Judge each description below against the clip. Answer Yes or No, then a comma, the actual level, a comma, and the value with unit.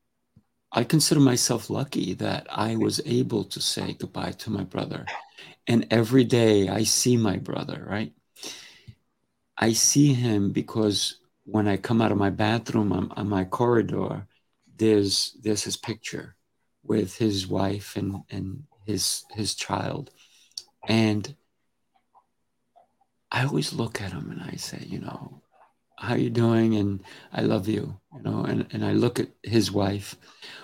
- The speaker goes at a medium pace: Yes, average, 150 wpm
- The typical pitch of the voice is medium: No, low, 110 Hz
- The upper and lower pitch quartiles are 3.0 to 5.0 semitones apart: No, narrow, 2.6 semitones